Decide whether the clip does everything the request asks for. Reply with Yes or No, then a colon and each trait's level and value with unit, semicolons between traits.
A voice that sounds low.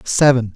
Yes: low, 120 Hz